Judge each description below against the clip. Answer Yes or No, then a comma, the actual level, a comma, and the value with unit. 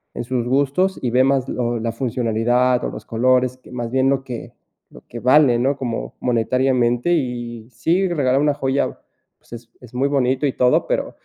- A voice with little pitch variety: Yes, narrow, 2.1 semitones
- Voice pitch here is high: No, low, 125 Hz